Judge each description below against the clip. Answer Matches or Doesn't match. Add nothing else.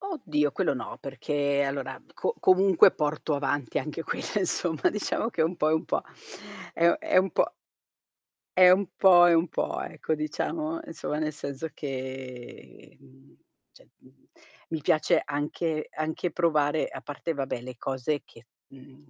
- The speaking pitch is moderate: Matches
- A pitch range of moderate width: Matches